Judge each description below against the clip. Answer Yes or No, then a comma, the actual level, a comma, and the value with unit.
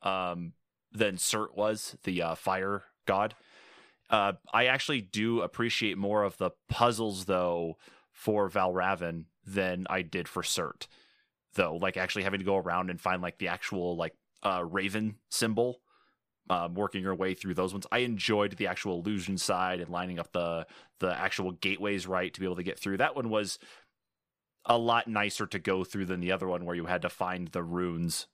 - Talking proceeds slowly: No, average, 185 wpm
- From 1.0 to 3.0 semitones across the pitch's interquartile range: Yes, narrow, 2.6 semitones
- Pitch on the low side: Yes, very low, 95 Hz